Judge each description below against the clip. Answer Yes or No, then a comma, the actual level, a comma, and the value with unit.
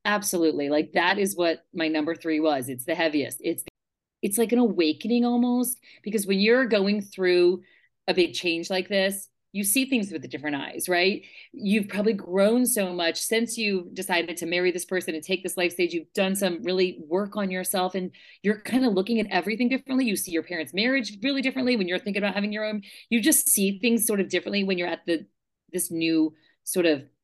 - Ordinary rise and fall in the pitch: Yes, average, 4.0 semitones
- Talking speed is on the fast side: Yes, fast, 215 wpm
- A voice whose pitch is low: No, high, 190 Hz